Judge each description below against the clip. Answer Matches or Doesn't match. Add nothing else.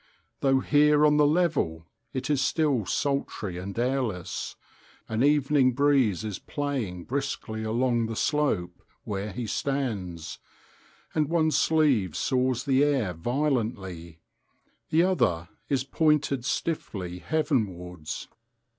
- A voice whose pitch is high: Doesn't match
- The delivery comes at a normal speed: Doesn't match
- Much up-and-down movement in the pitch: Matches